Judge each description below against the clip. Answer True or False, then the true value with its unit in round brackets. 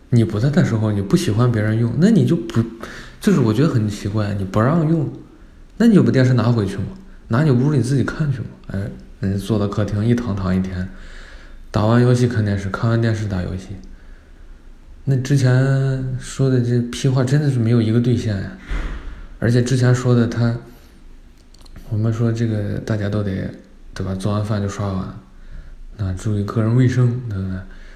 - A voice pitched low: True (110 Hz)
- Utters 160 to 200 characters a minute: False (270 characters per minute)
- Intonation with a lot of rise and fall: False (4.5 semitones)